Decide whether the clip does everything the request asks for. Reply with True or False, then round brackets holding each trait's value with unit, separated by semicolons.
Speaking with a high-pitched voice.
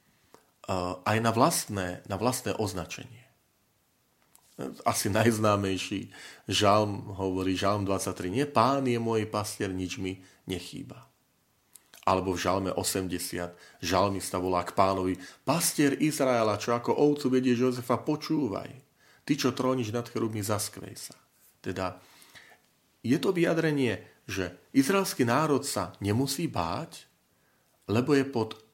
False (105 Hz)